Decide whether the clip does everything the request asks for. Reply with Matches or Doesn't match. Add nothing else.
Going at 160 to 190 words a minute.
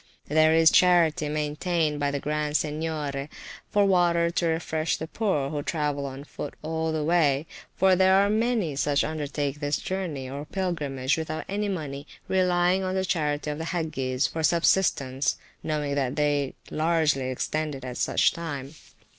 Matches